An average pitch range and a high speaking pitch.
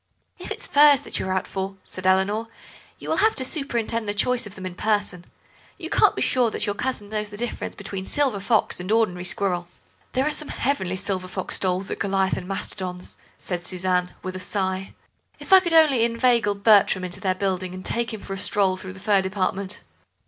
Yes: average, 3.6 semitones; high, 200 Hz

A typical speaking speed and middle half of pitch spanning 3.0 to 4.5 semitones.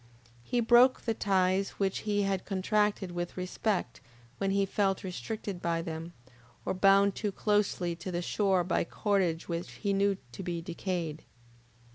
No: average, 155 wpm; narrow, 2.6 semitones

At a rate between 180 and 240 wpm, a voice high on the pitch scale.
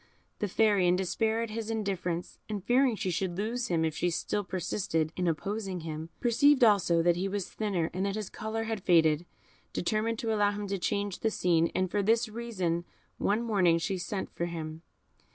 Yes: average, 195 wpm; high, 195 Hz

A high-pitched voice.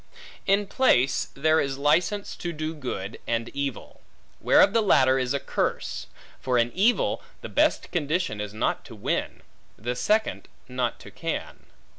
No: medium, 140 Hz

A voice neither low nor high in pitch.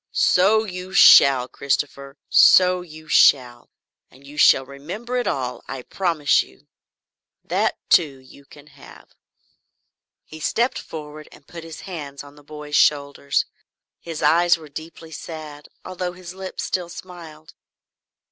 Yes: medium, 155 Hz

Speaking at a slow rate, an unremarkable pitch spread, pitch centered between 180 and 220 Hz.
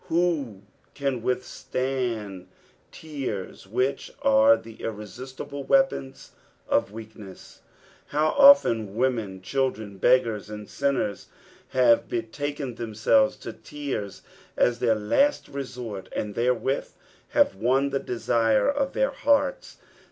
No: slow, 105 wpm; average, 4.6 semitones; low, 125 Hz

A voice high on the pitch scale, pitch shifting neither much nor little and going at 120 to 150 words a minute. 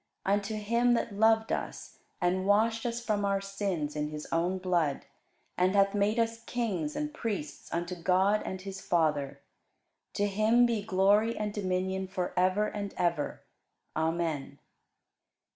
Yes: high, 195 Hz; average, 3.2 semitones; average, 145 wpm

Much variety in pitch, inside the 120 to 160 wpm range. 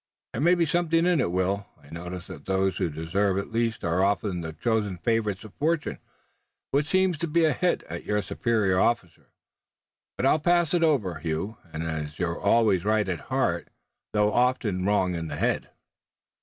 No: wide, 7.3 semitones; average, 185 wpm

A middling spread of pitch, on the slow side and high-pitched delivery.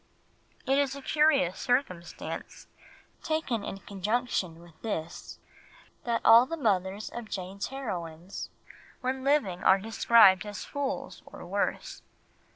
No: wide, 6.0 semitones; slow, 120 wpm; high, 220 Hz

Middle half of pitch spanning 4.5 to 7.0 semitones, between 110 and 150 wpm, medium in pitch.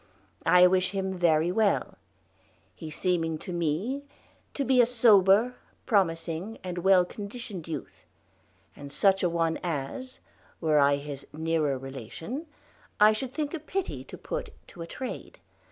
Yes: wide, 5.6 semitones; average, 145 wpm; medium, 180 Hz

